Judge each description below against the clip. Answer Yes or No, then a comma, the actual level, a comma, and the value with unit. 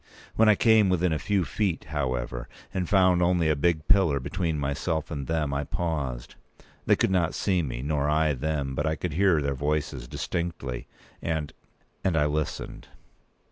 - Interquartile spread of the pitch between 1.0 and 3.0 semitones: No, average, 3.9 semitones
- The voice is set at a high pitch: No, very low, 80 Hz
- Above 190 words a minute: No, average, 175 wpm